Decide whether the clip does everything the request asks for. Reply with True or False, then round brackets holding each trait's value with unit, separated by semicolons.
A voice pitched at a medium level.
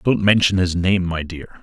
False (90 Hz)